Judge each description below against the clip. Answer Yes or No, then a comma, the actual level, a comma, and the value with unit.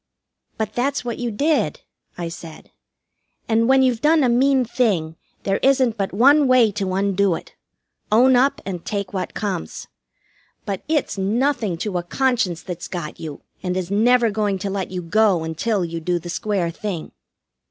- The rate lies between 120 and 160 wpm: No, average, 175 wpm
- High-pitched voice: Yes, high, 205 Hz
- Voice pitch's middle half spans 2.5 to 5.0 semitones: No, wide, 5.4 semitones